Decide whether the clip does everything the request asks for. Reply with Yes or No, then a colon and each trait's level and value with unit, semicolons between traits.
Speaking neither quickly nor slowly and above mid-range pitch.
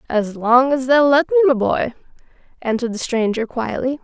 Yes: average, 180 wpm; very high, 255 Hz